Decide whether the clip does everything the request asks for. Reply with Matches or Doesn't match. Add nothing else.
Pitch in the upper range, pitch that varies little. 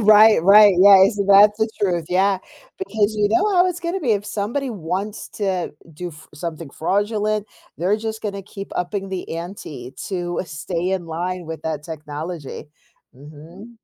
Doesn't match